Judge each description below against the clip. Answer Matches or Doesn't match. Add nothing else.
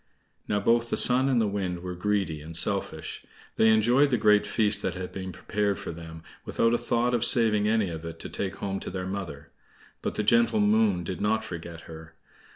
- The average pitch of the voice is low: Matches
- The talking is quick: Matches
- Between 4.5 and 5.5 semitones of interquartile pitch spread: Doesn't match